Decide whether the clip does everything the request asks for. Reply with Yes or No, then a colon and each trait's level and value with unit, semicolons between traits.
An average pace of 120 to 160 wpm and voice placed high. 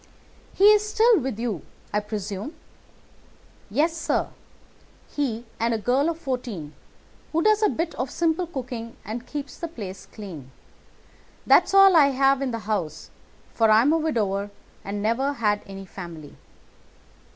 Yes: average, 150 wpm; high, 240 Hz